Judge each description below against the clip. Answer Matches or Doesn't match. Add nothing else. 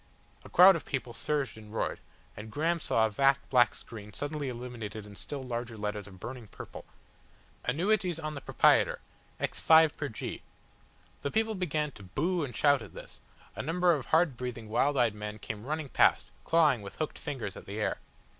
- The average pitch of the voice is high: Doesn't match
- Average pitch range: Doesn't match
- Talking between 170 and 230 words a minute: Matches